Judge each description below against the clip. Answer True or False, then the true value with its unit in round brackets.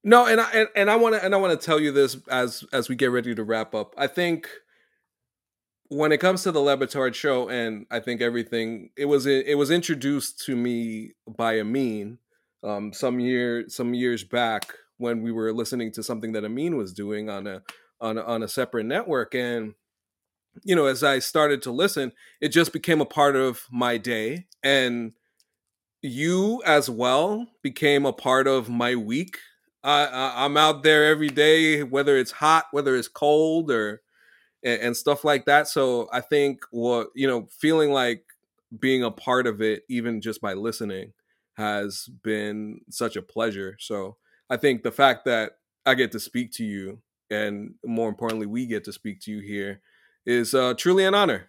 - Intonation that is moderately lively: True (4.3 semitones)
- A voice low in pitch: True (125 Hz)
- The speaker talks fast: False (185 wpm)